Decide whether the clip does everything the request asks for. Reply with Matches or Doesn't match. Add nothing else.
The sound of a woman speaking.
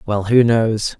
Doesn't match